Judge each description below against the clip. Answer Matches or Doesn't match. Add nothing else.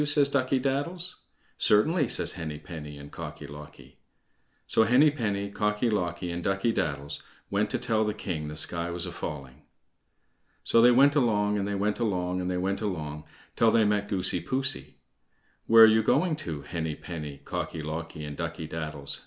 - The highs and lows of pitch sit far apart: Matches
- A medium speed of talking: Matches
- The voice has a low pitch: Matches